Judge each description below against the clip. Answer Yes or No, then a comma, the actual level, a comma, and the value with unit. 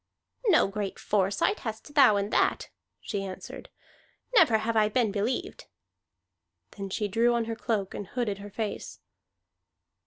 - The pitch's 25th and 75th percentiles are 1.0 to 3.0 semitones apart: Yes, narrow, 2.6 semitones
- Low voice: No, high, 215 Hz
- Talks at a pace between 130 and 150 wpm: Yes, average, 145 wpm